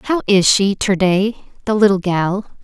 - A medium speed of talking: Yes, average, 160 wpm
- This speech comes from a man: No, female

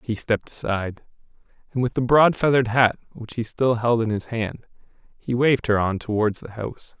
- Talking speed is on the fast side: No, average, 195 wpm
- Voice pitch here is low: Yes, low, 115 Hz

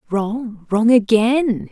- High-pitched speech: Yes, high, 225 Hz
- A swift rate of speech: No, slow, 105 wpm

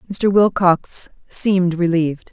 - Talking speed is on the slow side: Yes, slow, 105 wpm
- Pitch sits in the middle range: Yes, medium, 180 Hz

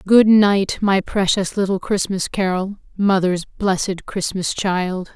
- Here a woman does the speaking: Yes, female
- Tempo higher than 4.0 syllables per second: No, 3.9 syllables/s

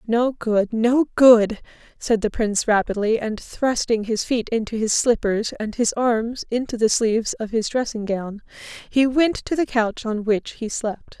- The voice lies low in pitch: No, high, 225 Hz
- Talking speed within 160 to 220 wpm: Yes, average, 180 wpm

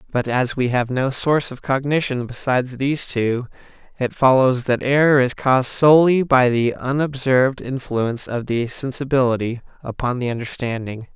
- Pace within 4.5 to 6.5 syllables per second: Yes, 5.1 syllables/s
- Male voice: Yes, male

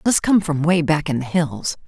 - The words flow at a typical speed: No, fast, 255 wpm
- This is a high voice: No, medium, 160 Hz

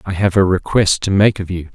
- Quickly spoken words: Yes, fast, 275 wpm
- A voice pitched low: Yes, very low, 95 Hz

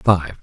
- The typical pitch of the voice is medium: No, very low, 85 Hz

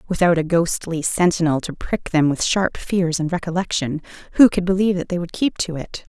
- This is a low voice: No, medium, 175 Hz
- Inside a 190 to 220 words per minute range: Yes, fast, 205 wpm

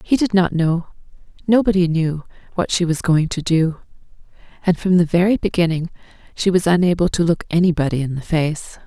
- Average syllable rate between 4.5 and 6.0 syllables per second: Yes, 5.5 syllables/s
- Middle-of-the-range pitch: Yes, medium, 170 Hz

